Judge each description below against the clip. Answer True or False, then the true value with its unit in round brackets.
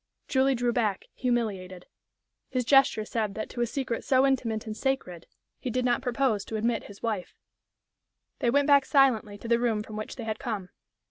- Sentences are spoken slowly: False (190 wpm)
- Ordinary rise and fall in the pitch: True (3.3 semitones)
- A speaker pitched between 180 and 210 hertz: False (235 Hz)